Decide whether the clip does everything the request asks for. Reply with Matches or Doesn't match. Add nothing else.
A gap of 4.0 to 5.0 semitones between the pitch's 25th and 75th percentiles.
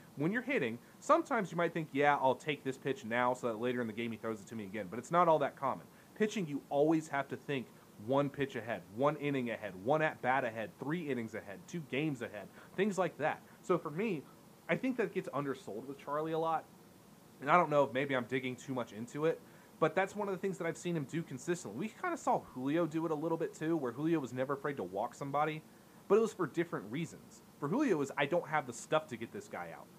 Matches